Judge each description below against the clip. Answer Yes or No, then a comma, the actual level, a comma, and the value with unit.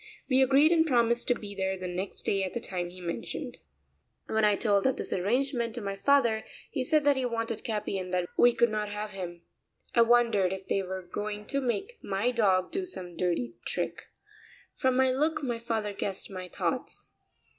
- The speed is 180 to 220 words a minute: Yes, average, 200 wpm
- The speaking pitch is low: No, high, 215 Hz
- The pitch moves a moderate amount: Yes, average, 4.8 semitones